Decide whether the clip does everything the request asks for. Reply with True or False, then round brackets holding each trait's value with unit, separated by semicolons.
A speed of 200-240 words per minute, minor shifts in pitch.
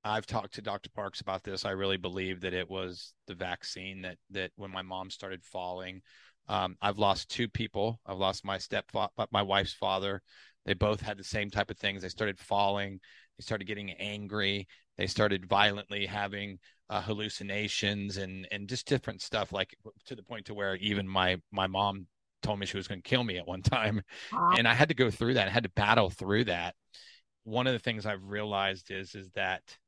True (205 wpm; 1.9 semitones)